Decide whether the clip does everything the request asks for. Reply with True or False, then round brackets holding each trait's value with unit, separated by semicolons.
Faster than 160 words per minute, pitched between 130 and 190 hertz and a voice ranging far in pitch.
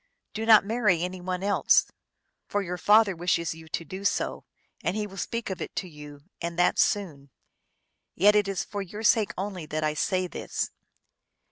False (190 wpm; 185 Hz; 3.5 semitones)